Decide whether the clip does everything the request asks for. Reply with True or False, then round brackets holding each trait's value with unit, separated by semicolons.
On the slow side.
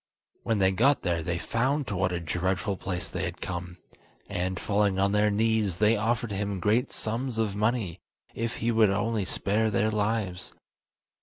False (175 wpm)